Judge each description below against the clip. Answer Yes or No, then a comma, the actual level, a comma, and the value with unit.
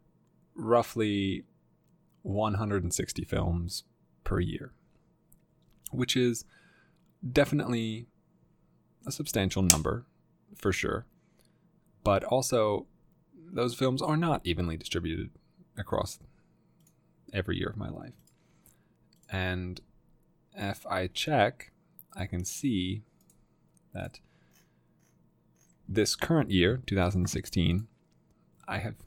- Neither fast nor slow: No, slow, 85 wpm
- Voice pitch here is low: Yes, very low, 95 Hz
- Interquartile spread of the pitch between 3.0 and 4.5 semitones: No, average, 5.1 semitones